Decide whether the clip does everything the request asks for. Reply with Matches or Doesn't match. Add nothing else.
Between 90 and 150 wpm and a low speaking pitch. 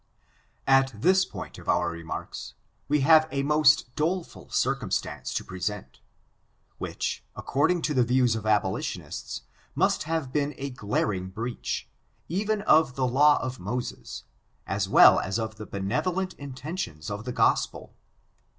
Matches